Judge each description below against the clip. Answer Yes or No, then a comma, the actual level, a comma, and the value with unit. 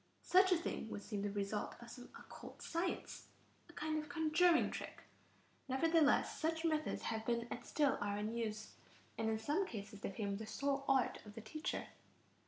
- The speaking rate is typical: Yes, average, 185 wpm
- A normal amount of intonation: No, wide, 6.5 semitones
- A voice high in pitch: Yes, high, 245 Hz